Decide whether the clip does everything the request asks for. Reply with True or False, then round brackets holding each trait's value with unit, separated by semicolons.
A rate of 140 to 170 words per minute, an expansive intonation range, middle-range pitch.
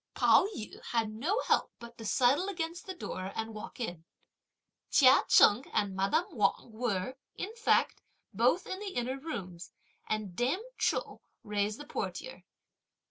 False (150 wpm; 7.7 semitones; 235 Hz)